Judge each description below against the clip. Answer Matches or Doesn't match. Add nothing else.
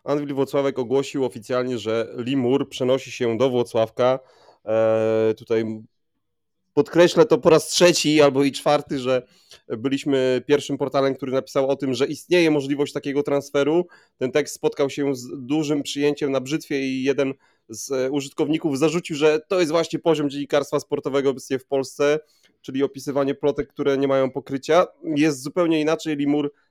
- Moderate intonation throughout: Doesn't match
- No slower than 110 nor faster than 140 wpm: Doesn't match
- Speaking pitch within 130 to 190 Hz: Matches